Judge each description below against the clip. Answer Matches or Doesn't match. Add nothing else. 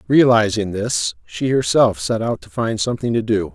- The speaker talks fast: Doesn't match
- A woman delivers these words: Doesn't match